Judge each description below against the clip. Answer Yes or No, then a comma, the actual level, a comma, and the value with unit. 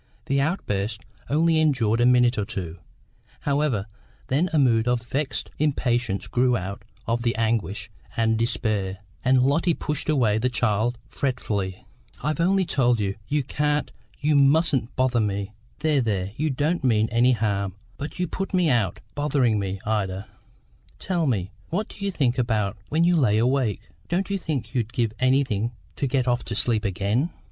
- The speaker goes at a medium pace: Yes, average, 170 wpm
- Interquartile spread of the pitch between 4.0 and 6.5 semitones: Yes, average, 5.3 semitones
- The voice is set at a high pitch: No, low, 125 Hz